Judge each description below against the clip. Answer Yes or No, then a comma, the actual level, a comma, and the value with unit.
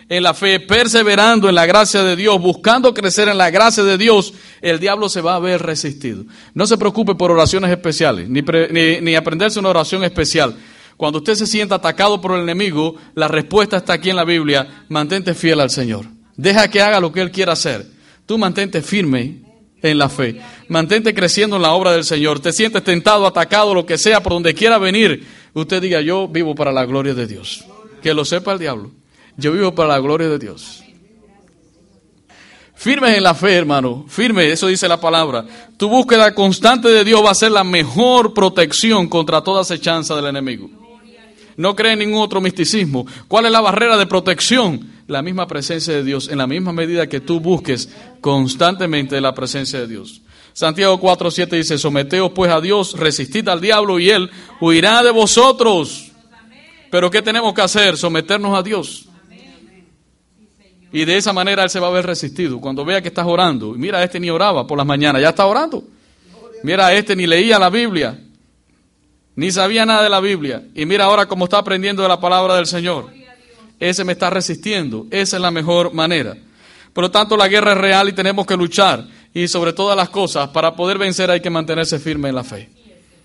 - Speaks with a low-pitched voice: No, medium, 180 Hz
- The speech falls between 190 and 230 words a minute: Yes, average, 195 wpm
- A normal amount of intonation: Yes, average, 4.1 semitones